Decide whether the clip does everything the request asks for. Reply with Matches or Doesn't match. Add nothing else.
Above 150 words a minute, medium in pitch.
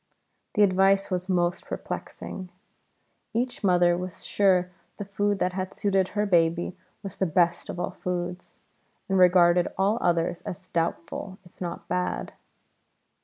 Doesn't match